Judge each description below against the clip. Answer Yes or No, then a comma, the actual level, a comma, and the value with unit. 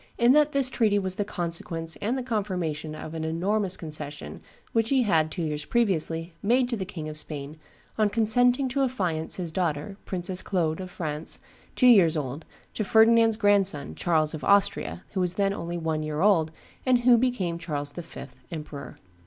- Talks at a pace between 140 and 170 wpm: No, average, 185 wpm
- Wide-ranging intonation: Yes, wide, 5.7 semitones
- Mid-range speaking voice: Yes, medium, 180 Hz